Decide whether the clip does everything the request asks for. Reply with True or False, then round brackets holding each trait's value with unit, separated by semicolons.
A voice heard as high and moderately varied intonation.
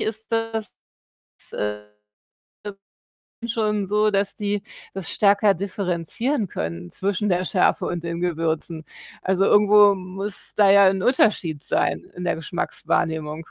True (195 Hz; 3.5 semitones)